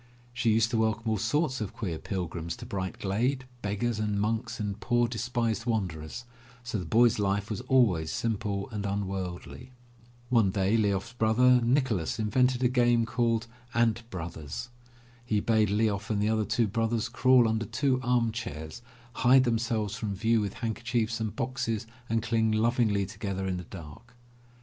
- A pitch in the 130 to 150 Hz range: No, low, 110 Hz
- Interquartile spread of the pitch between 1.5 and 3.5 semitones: Yes, average, 2.8 semitones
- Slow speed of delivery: No, average, 170 wpm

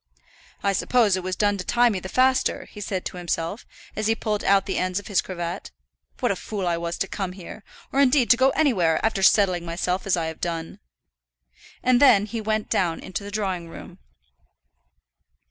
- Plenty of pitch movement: No, average, 3.4 semitones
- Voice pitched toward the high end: Yes, high, 195 Hz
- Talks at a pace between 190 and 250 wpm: Yes, average, 200 wpm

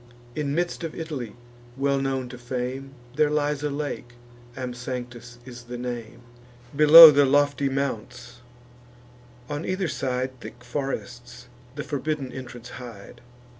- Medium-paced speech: No, slow, 130 wpm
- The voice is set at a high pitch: No, low, 130 Hz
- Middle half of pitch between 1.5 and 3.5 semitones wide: Yes, average, 2.9 semitones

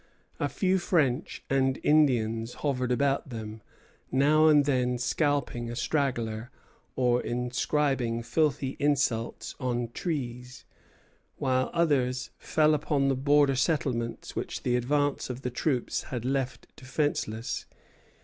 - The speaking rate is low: Yes, slow, 120 wpm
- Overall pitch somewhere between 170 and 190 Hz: No, low, 130 Hz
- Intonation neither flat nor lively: Yes, average, 3.0 semitones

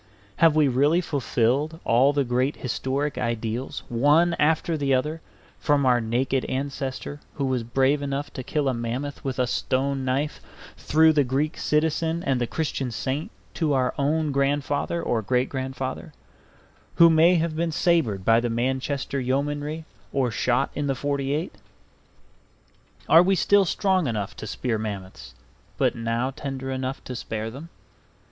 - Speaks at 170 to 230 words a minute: No, average, 155 wpm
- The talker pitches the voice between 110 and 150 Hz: Yes, low, 135 Hz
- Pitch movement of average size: Yes, average, 3.2 semitones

